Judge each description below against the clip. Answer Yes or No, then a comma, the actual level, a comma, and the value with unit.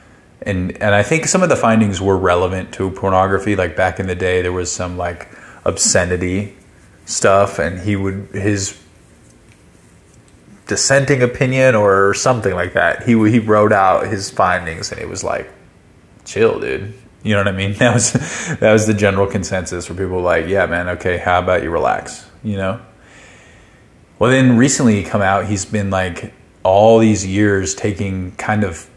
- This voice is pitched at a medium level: No, low, 100 Hz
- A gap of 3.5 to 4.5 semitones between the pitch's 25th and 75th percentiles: No, average, 2.9 semitones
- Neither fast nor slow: Yes, average, 175 wpm